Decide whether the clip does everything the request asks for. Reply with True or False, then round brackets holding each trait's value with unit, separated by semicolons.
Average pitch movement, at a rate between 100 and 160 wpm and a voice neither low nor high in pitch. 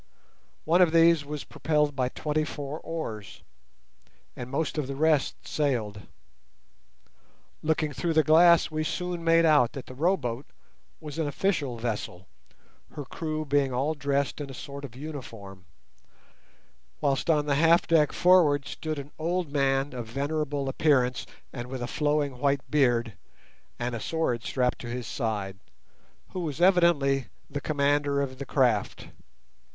True (3.6 semitones; 150 wpm; 145 Hz)